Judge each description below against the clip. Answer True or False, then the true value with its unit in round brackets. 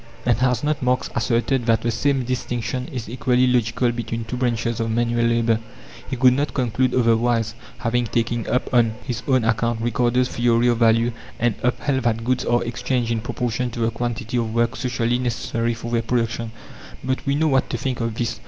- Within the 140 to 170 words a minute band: False (195 wpm)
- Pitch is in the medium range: False (120 Hz)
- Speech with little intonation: True (1.5 semitones)